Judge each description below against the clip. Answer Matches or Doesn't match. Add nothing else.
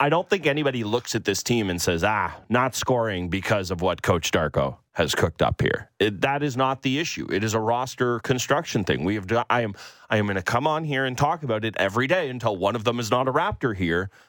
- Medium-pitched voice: Doesn't match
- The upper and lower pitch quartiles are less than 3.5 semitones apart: Doesn't match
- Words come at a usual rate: Doesn't match